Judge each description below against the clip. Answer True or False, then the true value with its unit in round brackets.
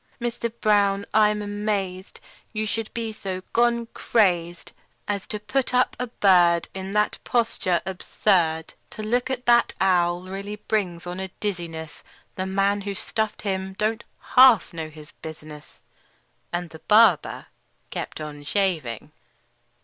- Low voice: False (195 Hz)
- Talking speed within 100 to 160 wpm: True (140 wpm)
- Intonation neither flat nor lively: True (3.7 semitones)